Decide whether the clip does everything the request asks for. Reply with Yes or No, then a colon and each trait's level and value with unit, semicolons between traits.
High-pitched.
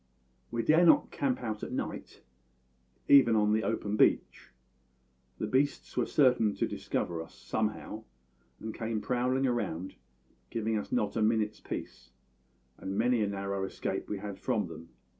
No: low, 110 Hz